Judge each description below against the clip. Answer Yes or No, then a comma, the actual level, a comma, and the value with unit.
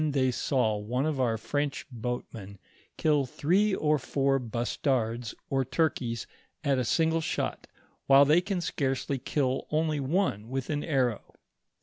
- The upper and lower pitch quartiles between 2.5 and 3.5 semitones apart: No, average, 3.9 semitones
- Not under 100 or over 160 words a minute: Yes, average, 155 wpm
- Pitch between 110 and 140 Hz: Yes, low, 135 Hz